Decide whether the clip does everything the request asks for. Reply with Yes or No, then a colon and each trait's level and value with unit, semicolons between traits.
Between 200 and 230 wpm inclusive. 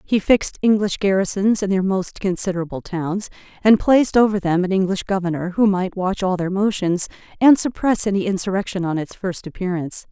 No: average, 180 wpm